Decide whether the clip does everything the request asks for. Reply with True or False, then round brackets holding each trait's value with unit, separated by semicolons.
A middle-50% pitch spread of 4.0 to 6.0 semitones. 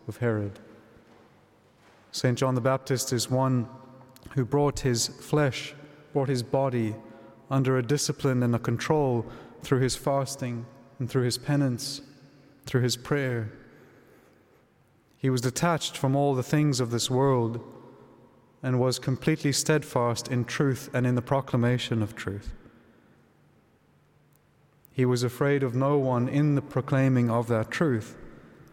False (2.8 semitones)